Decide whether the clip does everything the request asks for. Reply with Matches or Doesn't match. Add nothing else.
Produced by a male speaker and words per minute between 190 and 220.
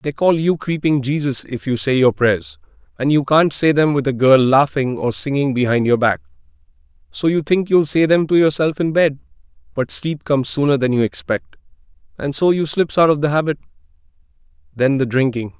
Matches